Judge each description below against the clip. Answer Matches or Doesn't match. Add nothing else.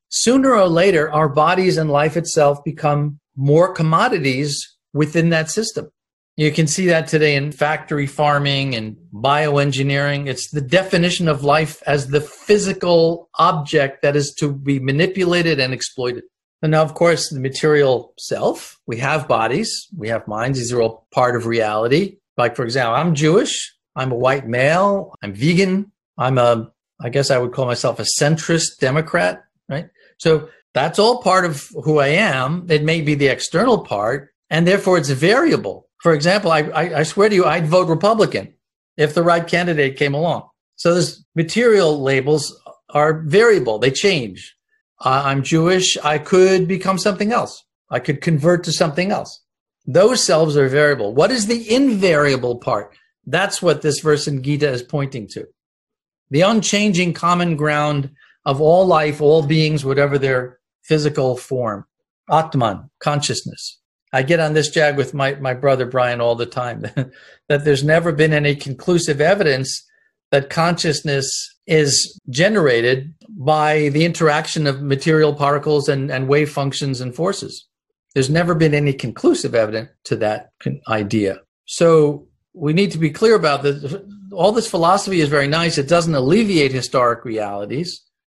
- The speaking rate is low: Doesn't match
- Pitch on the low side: Doesn't match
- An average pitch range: Matches